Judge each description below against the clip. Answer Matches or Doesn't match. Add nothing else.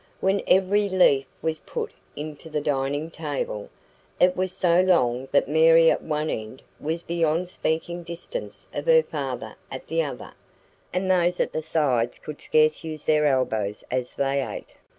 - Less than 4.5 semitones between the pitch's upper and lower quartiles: Matches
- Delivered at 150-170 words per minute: Matches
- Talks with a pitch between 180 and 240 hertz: Doesn't match